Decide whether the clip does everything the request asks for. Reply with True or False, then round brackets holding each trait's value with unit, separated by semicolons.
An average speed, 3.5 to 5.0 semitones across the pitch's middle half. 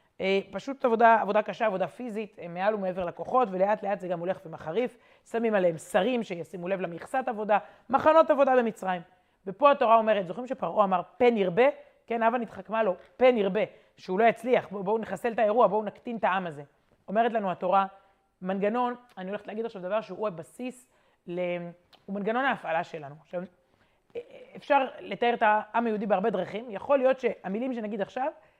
False (165 wpm; 4.4 semitones)